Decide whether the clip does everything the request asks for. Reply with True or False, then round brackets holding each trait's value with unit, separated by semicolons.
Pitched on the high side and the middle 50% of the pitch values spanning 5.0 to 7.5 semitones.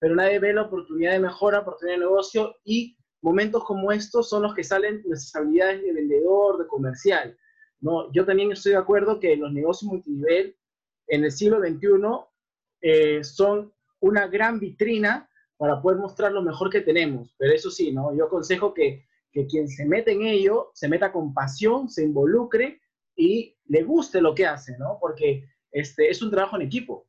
True (195 Hz; 5.3 semitones)